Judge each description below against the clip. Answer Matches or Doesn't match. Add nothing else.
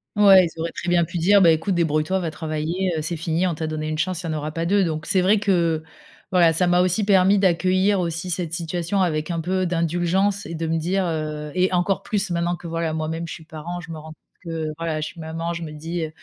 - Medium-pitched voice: Matches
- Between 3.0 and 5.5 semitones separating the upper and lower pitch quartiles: Doesn't match